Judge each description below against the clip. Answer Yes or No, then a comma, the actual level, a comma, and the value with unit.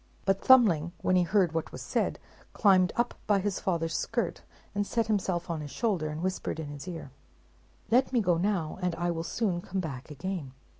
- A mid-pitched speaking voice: Yes, medium, 180 Hz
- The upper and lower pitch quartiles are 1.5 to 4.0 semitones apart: Yes, average, 3.6 semitones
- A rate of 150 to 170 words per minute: No, average, 200 wpm